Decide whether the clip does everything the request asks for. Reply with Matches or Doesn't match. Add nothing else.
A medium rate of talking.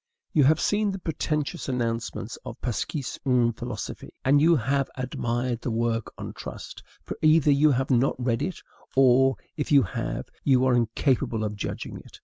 Matches